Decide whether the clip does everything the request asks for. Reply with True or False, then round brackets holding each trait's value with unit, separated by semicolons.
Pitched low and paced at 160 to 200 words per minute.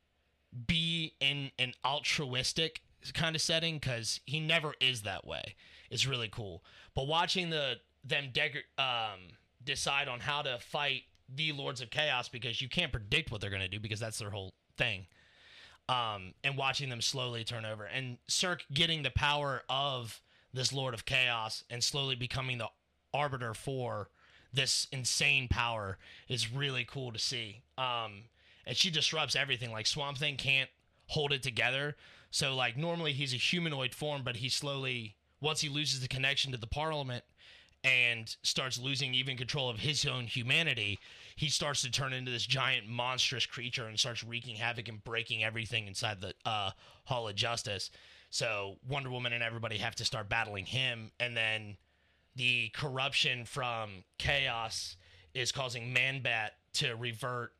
True (125 Hz; 165 wpm)